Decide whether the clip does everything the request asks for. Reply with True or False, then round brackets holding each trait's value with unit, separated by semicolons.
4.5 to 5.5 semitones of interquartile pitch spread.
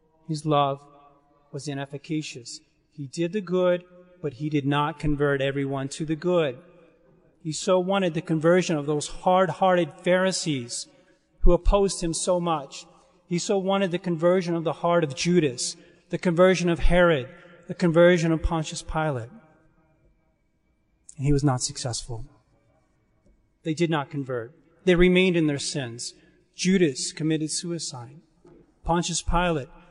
False (3.3 semitones)